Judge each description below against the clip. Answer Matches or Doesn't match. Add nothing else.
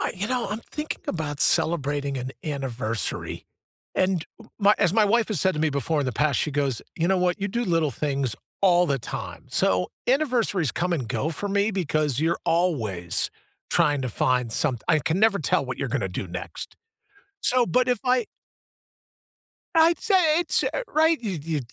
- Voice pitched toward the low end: Doesn't match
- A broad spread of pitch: Matches